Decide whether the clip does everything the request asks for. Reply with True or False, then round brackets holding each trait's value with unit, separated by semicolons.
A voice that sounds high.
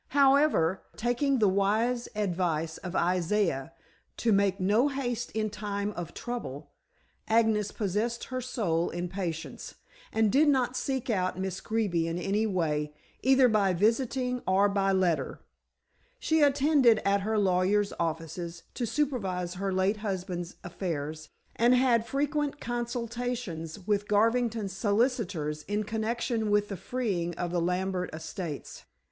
True (205 Hz)